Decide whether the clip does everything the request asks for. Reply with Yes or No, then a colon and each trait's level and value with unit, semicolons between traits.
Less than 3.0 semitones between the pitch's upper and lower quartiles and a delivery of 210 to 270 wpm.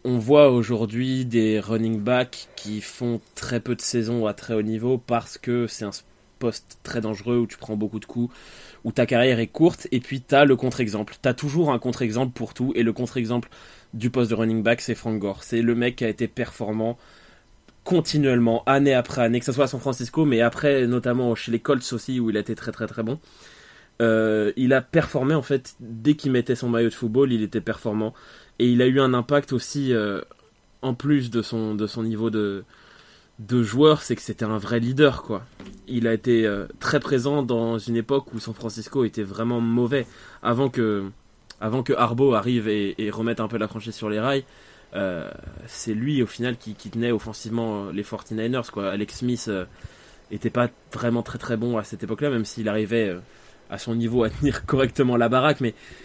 Yes: narrow, 2.5 semitones; average, 215 wpm